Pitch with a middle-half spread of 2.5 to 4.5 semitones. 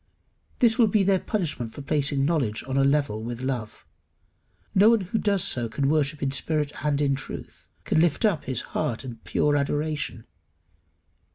Yes: average, 4.2 semitones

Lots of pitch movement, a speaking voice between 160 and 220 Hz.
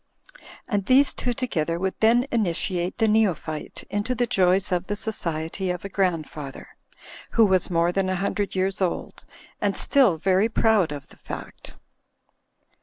No: average, 4.1 semitones; high, 190 Hz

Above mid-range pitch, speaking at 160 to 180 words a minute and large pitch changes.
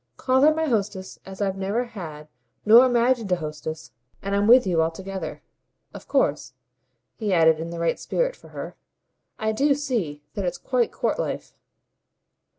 Yes: high, 200 Hz; average, 165 wpm; wide, 6.4 semitones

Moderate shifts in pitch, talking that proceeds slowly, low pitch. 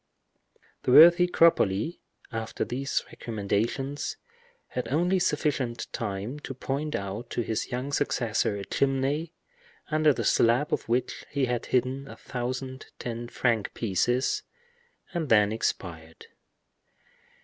Yes: average, 4.0 semitones; slow, 120 wpm; low, 125 Hz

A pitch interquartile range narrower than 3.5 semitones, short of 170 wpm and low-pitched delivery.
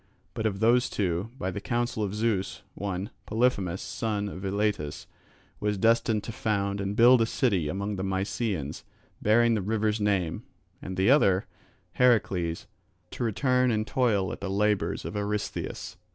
Yes: average, 2.8 semitones; average, 155 wpm; low, 105 Hz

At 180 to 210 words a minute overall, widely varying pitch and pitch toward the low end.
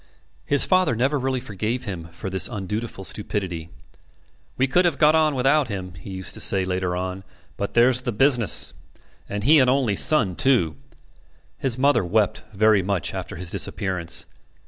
No: average, 170 wpm; wide, 6.0 semitones; low, 105 Hz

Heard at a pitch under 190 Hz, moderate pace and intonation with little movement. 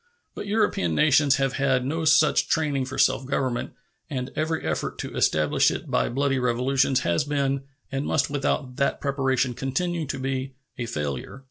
Yes: low, 135 Hz; average, 165 wpm; narrow, 2.2 semitones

